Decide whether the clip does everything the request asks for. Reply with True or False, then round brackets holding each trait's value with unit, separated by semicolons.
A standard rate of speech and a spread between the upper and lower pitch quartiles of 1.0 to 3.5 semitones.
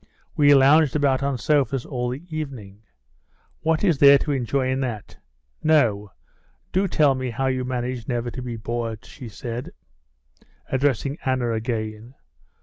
True (145 wpm; 3.0 semitones)